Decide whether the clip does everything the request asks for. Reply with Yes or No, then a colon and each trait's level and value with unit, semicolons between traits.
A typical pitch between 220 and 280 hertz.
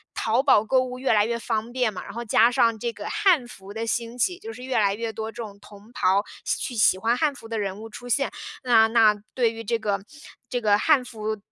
Yes: high, 230 Hz